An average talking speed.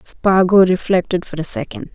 Yes: average, 155 wpm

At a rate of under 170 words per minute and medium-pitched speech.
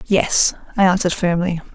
Yes: average, 140 wpm; medium, 180 Hz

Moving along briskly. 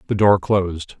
No: average, 180 wpm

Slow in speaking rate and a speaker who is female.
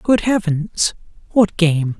No: slow, 90 wpm; male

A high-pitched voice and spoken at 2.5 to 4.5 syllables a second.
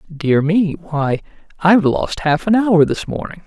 No: medium, 170 Hz; 4.4 syllables/s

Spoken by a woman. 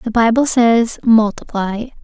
Yes: female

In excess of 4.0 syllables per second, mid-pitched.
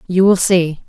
Yes: 4.2 syllables/s; medium, 180 Hz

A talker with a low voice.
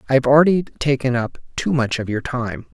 Yes: low, 130 Hz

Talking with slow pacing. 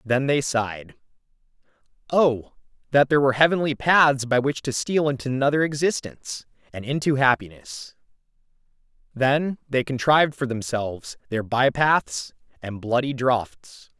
Yes: slow, 130 wpm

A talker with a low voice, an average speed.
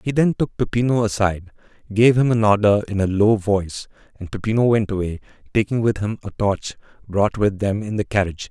Yes: low, 105 Hz; average, 195 wpm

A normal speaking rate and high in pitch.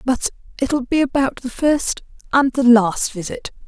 Yes: average, 165 wpm; very high, 255 Hz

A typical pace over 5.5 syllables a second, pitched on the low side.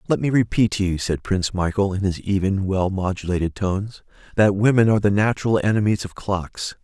Yes: 5.7 syllables/s; low, 100 Hz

